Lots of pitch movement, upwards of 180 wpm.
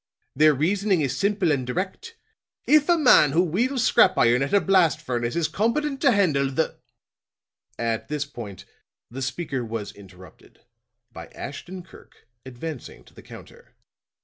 No: wide, 7.6 semitones; average, 155 wpm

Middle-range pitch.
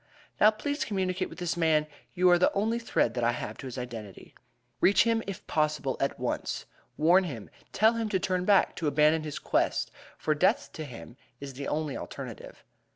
Yes: medium, 160 Hz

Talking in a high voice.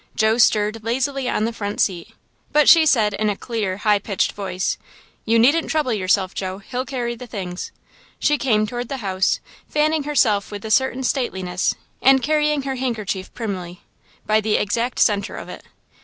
Yes: high, 220 Hz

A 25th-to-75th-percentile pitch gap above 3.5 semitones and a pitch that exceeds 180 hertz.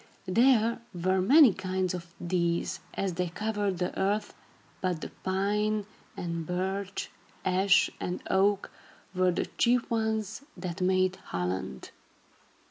No: narrow, 2.6 semitones; high, 190 Hz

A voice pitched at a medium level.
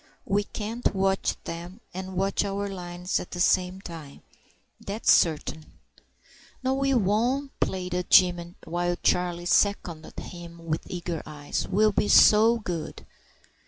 Yes: medium, 180 Hz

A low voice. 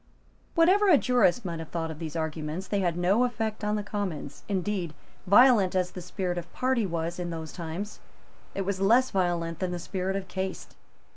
No: medium, 185 Hz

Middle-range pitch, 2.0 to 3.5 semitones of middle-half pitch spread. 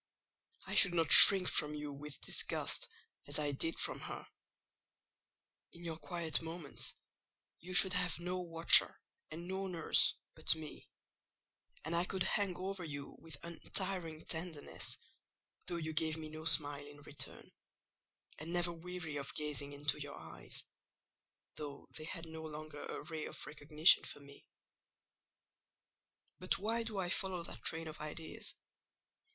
Yes: medium, 160 Hz; average, 2.9 semitones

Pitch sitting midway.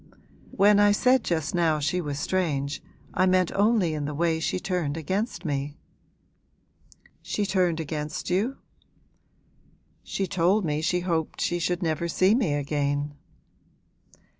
Yes: medium, 170 Hz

